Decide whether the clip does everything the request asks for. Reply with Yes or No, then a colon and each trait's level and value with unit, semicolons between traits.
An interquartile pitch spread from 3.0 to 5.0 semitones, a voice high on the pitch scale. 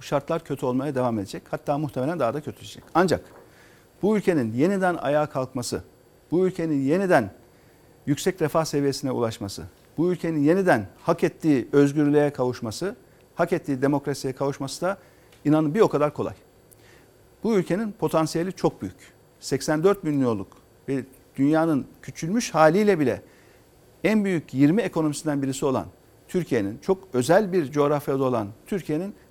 No: average, 4.7 semitones; medium, 145 Hz